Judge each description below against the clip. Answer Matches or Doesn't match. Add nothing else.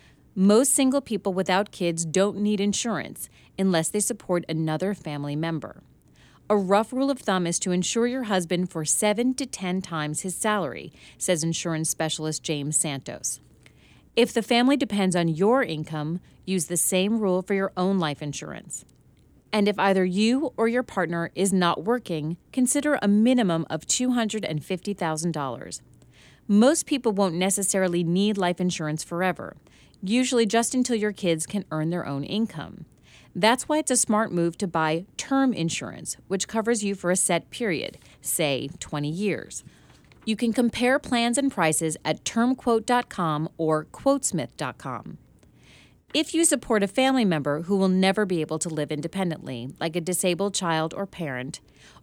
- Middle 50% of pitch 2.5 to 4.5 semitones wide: Doesn't match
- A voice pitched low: Doesn't match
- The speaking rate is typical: Matches